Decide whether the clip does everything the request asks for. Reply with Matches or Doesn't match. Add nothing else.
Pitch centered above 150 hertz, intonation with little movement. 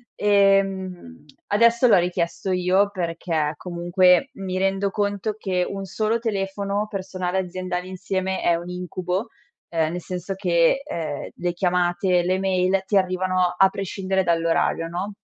Matches